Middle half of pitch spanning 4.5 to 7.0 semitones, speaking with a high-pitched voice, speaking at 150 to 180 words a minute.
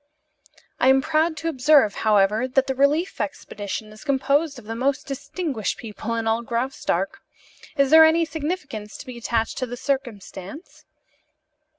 Yes: average, 4.9 semitones; very high, 265 Hz; average, 155 wpm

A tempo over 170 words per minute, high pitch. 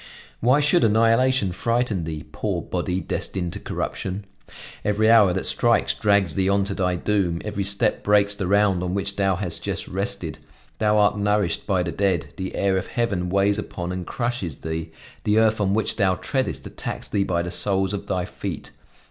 No: average, 190 wpm; low, 100 Hz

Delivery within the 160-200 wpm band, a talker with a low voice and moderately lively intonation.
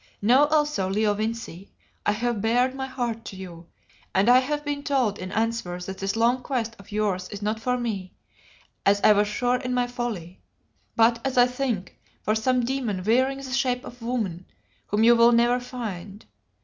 No: average, 190 wpm; high, 230 Hz; average, 3.6 semitones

